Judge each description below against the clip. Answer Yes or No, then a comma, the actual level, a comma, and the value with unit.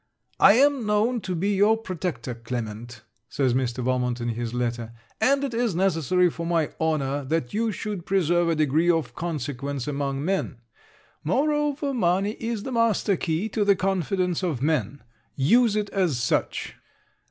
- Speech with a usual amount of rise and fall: No, wide, 7.3 semitones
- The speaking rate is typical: Yes, average, 160 wpm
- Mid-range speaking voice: Yes, medium, 170 Hz